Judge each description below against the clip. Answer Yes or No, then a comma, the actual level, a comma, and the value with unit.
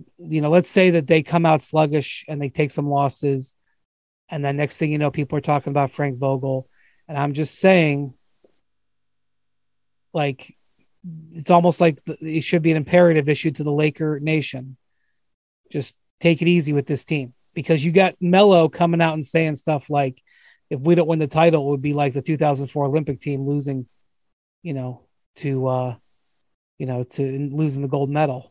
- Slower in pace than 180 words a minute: No, average, 185 wpm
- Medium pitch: Yes, medium, 150 Hz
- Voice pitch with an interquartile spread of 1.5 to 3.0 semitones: Yes, narrow, 2.6 semitones